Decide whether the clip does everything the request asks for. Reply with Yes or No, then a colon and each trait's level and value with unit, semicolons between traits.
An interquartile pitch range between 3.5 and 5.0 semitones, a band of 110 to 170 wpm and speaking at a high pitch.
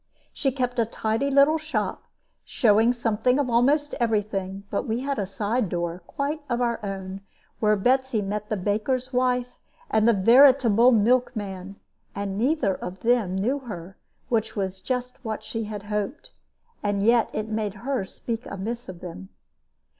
Yes: average, 3.8 semitones; average, 160 wpm; high, 220 Hz